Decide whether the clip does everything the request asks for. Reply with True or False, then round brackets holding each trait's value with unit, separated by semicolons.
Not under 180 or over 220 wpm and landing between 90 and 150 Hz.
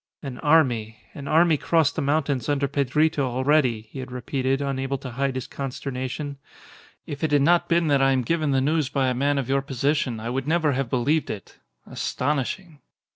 True (190 wpm; 140 Hz)